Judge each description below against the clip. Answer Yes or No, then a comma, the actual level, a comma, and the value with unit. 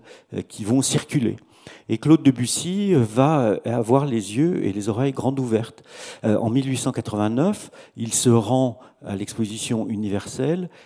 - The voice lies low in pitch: Yes, low, 125 Hz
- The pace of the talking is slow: Yes, slow, 125 wpm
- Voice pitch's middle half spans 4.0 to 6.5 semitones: No, average, 3.5 semitones